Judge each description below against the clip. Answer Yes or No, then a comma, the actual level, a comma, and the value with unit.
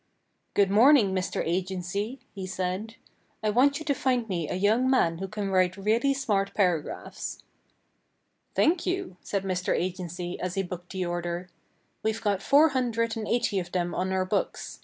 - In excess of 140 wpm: Yes, average, 170 wpm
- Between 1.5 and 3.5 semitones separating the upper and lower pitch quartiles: No, average, 4.1 semitones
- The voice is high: Yes, high, 195 Hz